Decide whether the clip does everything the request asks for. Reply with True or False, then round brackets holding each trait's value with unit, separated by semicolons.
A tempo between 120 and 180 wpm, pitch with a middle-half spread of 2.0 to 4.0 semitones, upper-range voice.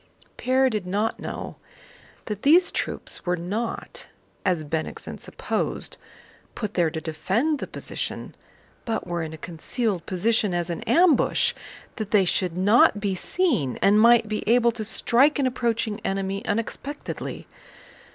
False (140 wpm; 4.8 semitones; 210 Hz)